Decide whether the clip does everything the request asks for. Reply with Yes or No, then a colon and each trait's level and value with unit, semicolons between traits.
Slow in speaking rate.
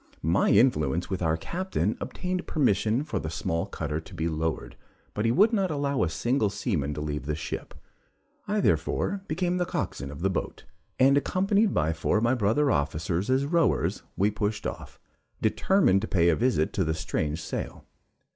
No: average, 180 wpm